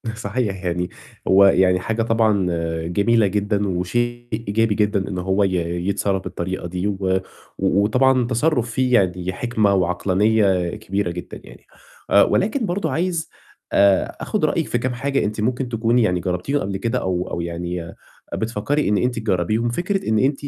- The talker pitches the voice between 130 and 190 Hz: No, low, 105 Hz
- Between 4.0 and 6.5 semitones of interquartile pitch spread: Yes, average, 4.3 semitones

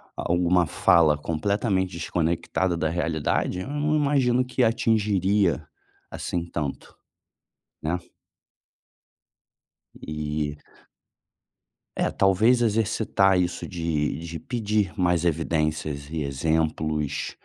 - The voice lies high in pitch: No, very low, 85 Hz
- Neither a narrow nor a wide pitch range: Yes, average, 5.0 semitones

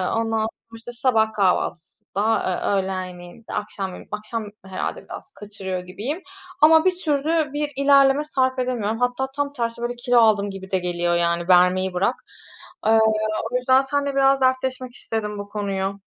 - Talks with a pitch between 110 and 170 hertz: No, high, 225 Hz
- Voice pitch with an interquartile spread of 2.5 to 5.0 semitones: No, wide, 5.4 semitones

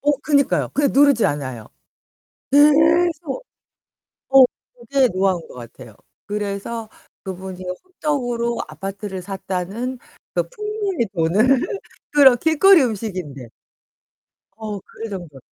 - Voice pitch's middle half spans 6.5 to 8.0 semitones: Yes, wide, 7.3 semitones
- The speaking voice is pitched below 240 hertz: Yes, high, 230 Hz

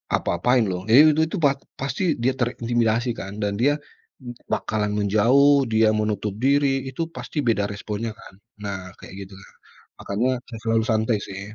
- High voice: No, low, 115 Hz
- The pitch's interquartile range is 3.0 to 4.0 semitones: Yes, average, 3.7 semitones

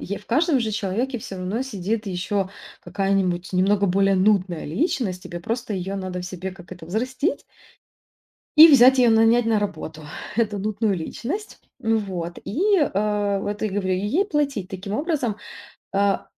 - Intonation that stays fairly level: No, average, 3.9 semitones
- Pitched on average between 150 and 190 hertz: No, high, 205 Hz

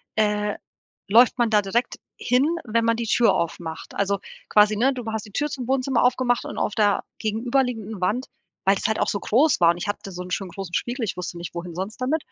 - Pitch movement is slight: No, average, 4.0 semitones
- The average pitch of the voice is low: No, high, 215 Hz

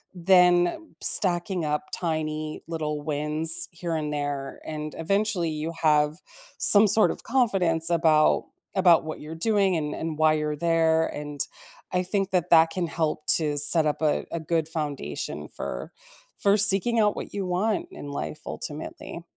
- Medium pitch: Yes, medium, 165 Hz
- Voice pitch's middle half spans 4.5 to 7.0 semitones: No, average, 3.0 semitones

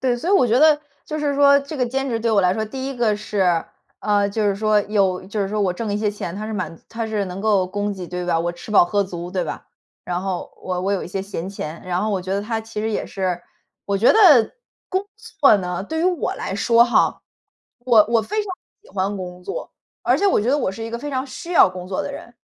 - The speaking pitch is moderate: No, high, 210 Hz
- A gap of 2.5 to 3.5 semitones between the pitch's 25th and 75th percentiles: No, average, 4.5 semitones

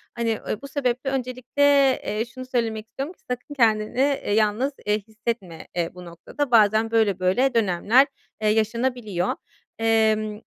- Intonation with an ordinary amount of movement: Yes, average, 3.2 semitones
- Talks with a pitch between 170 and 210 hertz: No, high, 225 Hz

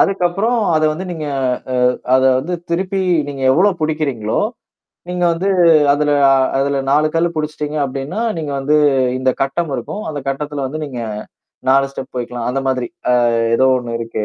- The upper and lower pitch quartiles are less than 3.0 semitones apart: No, average, 4.2 semitones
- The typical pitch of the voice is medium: Yes, medium, 145 Hz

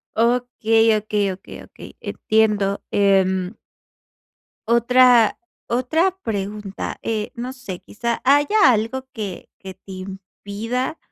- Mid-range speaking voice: No, high, 220 Hz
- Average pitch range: Yes, average, 3.8 semitones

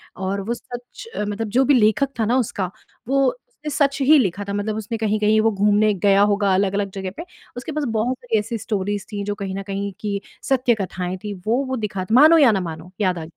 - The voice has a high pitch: Yes, high, 210 Hz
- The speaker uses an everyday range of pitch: Yes, average, 3.7 semitones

